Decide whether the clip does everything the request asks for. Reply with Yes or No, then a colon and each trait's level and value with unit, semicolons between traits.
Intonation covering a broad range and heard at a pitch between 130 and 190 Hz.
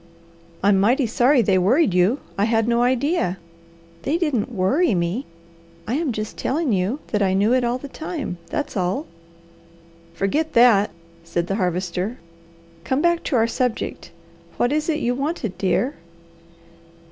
No: wide, 6.6 semitones; high, 235 Hz